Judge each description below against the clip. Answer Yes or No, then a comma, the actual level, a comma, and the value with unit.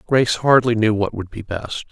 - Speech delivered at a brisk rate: Yes, fast, 220 wpm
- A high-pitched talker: No, low, 110 Hz